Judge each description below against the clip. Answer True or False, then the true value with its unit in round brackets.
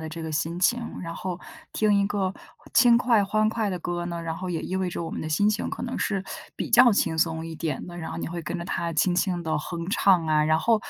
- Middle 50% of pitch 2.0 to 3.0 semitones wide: False (3.8 semitones)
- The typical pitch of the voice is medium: True (175 Hz)